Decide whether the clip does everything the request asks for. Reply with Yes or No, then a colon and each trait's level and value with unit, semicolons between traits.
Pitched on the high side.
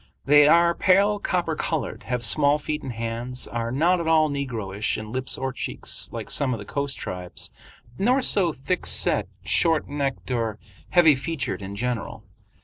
No: medium, 140 Hz